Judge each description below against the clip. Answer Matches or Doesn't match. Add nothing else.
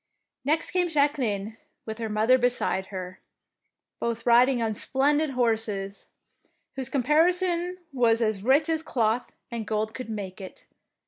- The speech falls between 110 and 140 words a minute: Matches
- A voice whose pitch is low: Doesn't match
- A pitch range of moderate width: Matches